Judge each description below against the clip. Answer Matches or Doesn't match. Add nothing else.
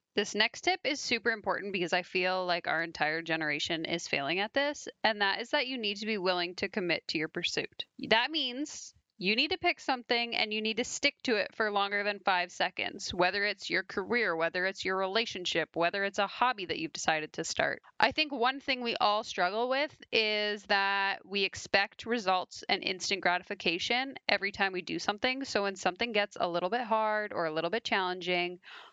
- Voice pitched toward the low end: Doesn't match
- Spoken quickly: Matches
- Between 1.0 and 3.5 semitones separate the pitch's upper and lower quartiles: Doesn't match